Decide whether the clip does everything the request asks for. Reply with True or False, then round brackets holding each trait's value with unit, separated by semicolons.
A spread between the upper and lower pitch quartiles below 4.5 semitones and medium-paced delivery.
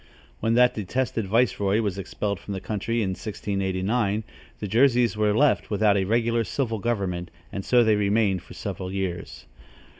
True (3.0 semitones; 160 wpm)